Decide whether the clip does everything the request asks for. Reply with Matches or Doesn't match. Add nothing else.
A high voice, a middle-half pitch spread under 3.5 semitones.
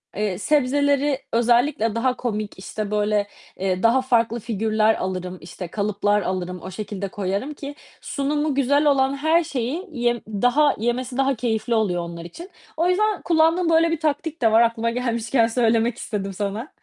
Doesn't match